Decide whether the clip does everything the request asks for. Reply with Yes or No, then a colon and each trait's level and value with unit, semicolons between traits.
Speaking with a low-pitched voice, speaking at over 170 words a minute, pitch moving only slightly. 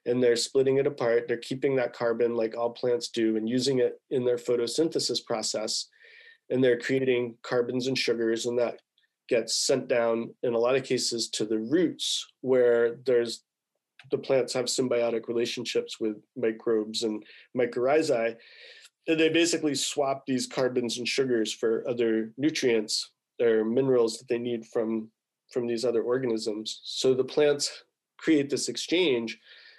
No: low, 120 Hz; average, 155 wpm; narrow, 2.3 semitones